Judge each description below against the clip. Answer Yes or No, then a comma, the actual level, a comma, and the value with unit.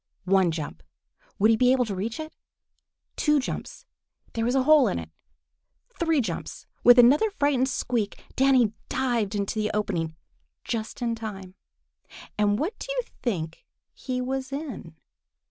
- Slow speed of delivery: No, average, 150 wpm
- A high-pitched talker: Yes, high, 235 Hz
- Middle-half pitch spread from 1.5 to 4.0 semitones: No, average, 4.9 semitones